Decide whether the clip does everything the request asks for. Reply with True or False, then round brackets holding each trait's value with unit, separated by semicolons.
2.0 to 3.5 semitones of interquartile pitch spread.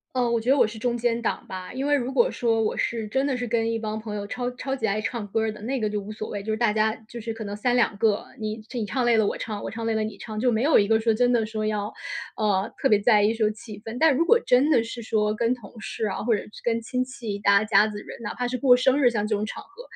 True (2.4 semitones)